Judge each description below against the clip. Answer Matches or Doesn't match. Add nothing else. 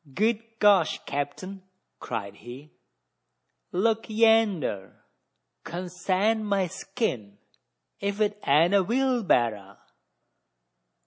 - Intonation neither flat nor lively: Doesn't match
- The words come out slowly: Matches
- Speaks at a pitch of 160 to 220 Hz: Matches